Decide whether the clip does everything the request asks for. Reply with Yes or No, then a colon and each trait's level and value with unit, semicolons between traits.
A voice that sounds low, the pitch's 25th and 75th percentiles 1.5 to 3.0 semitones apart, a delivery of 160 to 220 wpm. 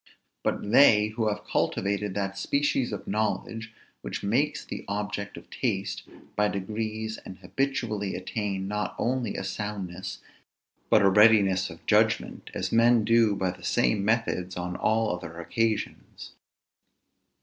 No: low, 105 Hz; narrow, 2.5 semitones; average, 140 wpm